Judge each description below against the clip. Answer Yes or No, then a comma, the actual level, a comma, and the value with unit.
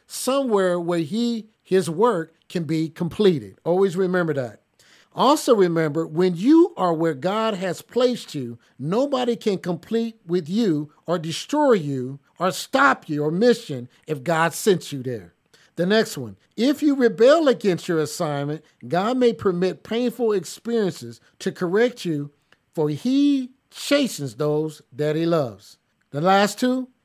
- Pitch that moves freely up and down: Yes, wide, 7.0 semitones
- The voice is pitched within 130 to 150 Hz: No, medium, 180 Hz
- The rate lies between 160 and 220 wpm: No, average, 145 wpm